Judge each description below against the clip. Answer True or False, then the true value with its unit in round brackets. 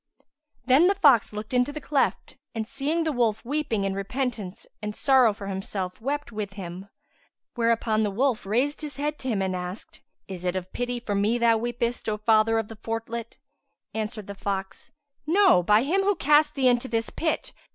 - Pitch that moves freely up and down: False (4.8 semitones)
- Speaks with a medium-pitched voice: False (225 Hz)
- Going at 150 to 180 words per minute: False (190 wpm)